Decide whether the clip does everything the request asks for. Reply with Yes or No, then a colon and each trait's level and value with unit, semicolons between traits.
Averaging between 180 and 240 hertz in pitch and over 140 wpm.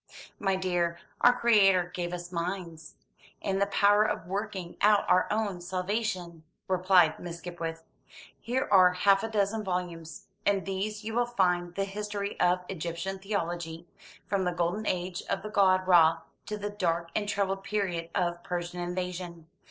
Yes: medium, 185 Hz; average, 160 wpm